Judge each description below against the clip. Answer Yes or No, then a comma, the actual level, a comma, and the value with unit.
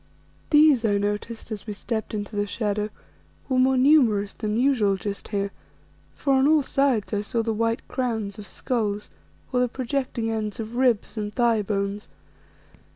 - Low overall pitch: No, high, 225 Hz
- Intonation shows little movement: No, average, 3.5 semitones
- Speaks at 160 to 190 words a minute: Yes, average, 165 wpm